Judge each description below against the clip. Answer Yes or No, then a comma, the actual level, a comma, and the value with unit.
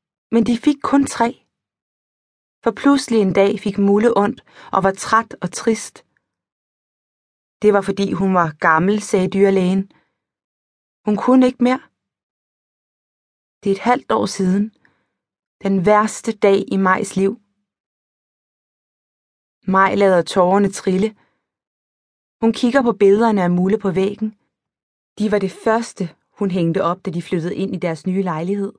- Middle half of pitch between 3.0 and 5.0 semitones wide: No, narrow, 2.6 semitones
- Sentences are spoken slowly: Yes, slow, 140 wpm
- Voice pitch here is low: No, high, 200 Hz